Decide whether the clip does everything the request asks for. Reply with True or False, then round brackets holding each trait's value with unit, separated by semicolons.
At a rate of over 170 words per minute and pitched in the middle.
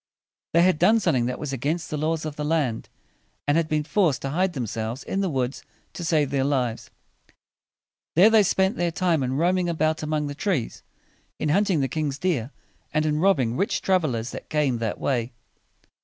True (200 wpm; 155 Hz)